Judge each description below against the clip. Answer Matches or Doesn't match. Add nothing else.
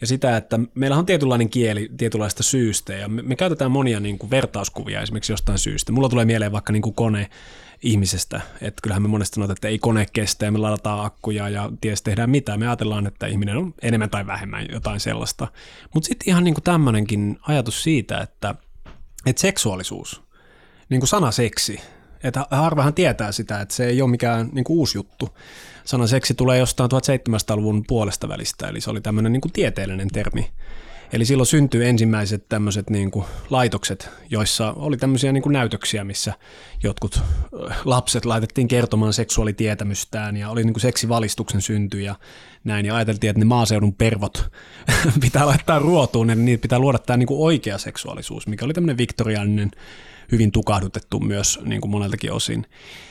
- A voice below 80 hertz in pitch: Doesn't match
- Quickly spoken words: Matches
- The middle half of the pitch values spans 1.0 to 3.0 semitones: Doesn't match